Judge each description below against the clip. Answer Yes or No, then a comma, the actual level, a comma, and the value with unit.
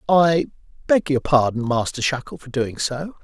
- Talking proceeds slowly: No, average, 150 wpm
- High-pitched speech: No, medium, 140 Hz